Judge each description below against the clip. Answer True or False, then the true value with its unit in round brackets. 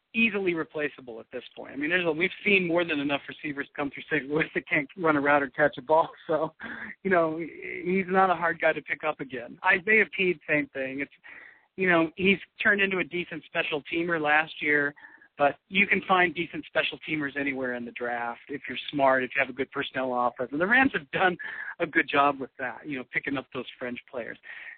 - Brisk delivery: True (230 wpm)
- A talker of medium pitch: True (155 Hz)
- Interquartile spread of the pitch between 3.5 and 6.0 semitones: True (4.0 semitones)